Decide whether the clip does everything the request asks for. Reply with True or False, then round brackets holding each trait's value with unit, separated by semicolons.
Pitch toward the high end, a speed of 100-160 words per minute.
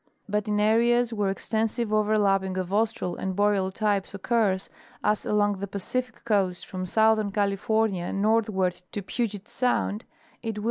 True (210 Hz; 150 wpm)